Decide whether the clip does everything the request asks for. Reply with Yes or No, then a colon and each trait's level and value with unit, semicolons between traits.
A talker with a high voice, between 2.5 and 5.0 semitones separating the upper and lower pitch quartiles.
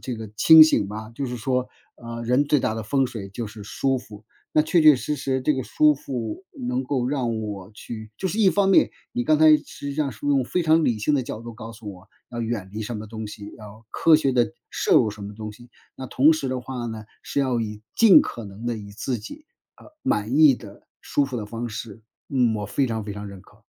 No: low, 120 Hz; average, 4.4 semitones